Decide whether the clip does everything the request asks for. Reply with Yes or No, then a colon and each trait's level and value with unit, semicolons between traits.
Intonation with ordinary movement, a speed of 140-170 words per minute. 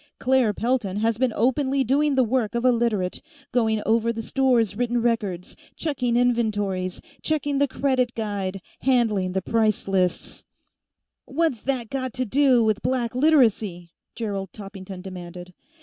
Yes: average, 4.3 semitones; average, 150 wpm